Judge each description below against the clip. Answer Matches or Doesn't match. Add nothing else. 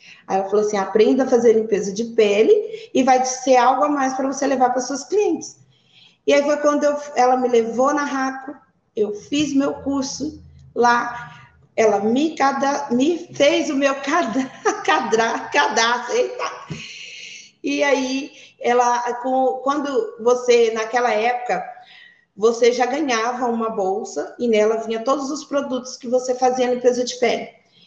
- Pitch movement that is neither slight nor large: Matches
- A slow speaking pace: Doesn't match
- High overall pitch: Matches